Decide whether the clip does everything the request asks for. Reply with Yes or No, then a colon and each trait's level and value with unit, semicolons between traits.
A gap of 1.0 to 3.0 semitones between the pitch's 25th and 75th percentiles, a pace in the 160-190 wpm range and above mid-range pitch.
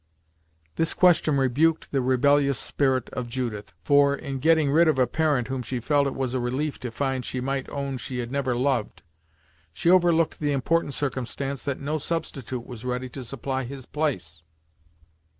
No: narrow, 2.5 semitones; average, 175 wpm; low, 135 Hz